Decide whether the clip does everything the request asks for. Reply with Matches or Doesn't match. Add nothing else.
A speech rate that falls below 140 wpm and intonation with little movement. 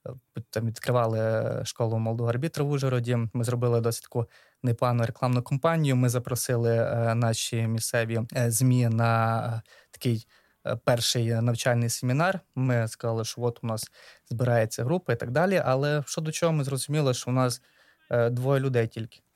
Doesn't match